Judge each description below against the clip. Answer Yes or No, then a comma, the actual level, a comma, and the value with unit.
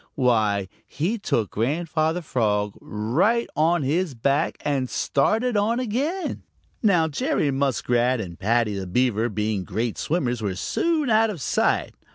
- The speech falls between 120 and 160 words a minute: Yes, average, 140 wpm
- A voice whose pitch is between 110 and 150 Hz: Yes, low, 135 Hz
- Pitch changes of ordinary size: No, wide, 8.7 semitones